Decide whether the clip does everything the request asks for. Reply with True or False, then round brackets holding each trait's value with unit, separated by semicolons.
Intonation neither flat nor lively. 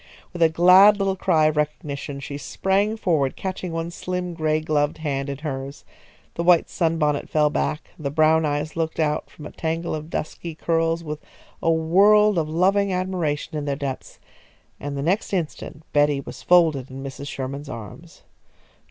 True (3.0 semitones)